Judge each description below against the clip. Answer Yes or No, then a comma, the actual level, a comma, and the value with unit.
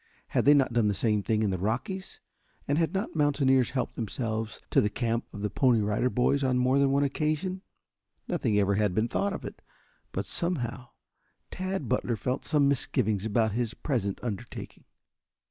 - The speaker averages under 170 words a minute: No, average, 180 wpm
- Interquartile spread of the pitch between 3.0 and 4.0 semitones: No, average, 4.5 semitones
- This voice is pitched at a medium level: No, low, 125 Hz